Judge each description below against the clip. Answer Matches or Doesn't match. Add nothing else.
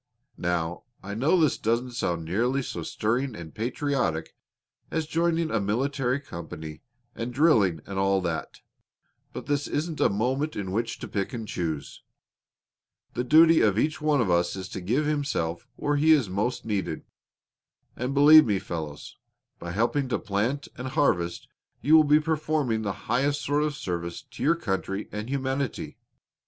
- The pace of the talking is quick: Doesn't match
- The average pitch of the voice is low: Matches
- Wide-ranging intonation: Matches